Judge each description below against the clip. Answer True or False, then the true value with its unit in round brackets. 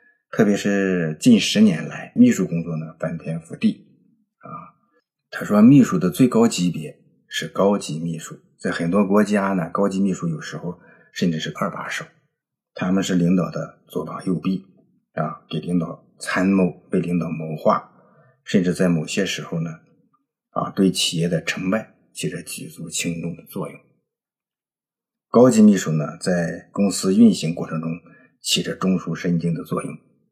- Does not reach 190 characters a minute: False (230 characters per minute)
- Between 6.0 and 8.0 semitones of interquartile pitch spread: False (5.4 semitones)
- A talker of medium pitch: False (90 Hz)